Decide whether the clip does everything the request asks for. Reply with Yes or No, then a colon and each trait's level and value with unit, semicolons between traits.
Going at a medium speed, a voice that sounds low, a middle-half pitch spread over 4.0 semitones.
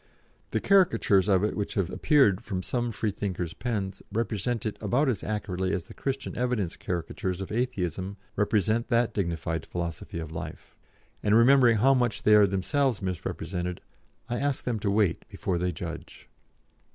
Yes: average, 160 wpm; low, 105 Hz; average, 4.7 semitones